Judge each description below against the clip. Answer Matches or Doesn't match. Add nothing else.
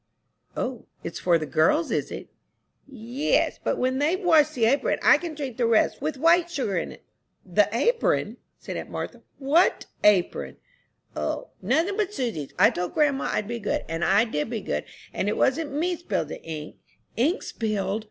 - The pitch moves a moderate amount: Doesn't match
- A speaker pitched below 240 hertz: Doesn't match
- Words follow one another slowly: Doesn't match